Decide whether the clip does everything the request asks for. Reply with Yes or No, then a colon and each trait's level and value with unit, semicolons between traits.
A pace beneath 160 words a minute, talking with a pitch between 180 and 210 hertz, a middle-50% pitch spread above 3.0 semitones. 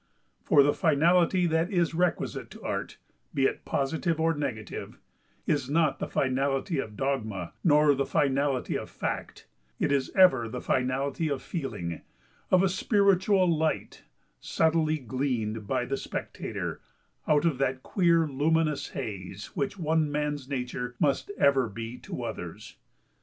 No: average, 140 wpm; medium, 140 Hz; average, 4.0 semitones